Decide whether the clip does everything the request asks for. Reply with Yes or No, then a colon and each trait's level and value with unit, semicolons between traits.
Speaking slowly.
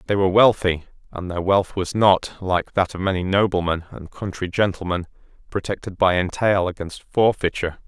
No: average, 160 wpm